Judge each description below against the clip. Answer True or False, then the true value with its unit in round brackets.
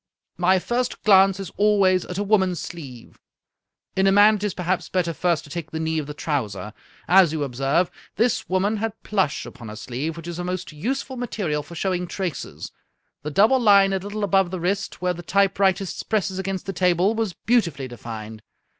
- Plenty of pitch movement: False (3.8 semitones)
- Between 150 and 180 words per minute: False (200 wpm)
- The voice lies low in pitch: False (185 Hz)